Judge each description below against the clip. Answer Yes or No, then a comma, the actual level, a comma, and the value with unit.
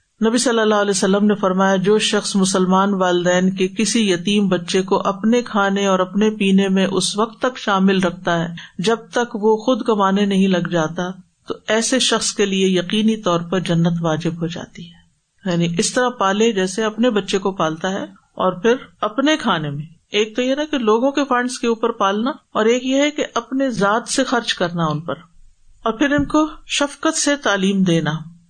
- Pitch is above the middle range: Yes, high, 205 Hz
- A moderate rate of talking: No, fast, 200 wpm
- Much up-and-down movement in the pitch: No, average, 3.9 semitones